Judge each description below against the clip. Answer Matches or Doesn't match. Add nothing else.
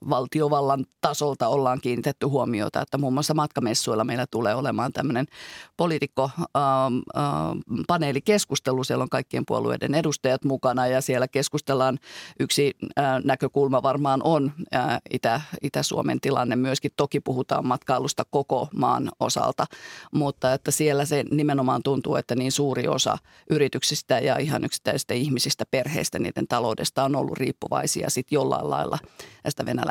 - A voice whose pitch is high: Doesn't match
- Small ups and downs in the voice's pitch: Matches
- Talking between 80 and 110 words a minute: Doesn't match